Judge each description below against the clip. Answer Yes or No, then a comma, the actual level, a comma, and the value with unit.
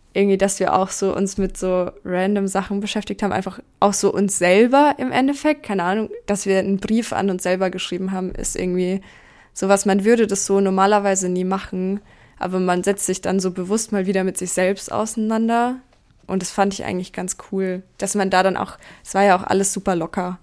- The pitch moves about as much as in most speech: No, narrow, 1.6 semitones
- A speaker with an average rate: No, fast, 210 wpm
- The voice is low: No, high, 195 Hz